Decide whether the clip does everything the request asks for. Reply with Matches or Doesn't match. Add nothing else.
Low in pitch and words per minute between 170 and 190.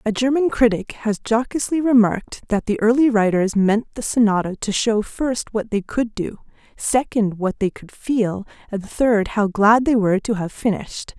Doesn't match